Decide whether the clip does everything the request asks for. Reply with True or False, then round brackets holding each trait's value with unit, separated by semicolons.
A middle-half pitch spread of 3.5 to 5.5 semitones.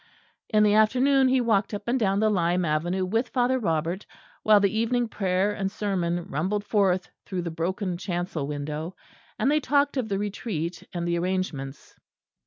True (4.0 semitones)